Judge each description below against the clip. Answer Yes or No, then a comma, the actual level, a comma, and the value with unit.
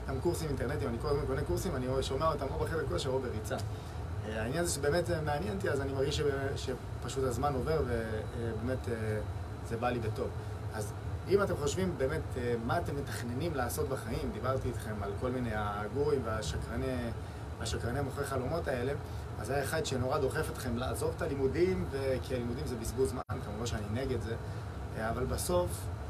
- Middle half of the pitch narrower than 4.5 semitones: Yes, average, 3.8 semitones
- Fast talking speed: Yes, fast, 165 wpm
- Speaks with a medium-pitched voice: No, low, 115 Hz